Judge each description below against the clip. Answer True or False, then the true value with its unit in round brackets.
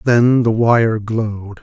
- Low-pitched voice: True (115 Hz)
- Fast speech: False (145 wpm)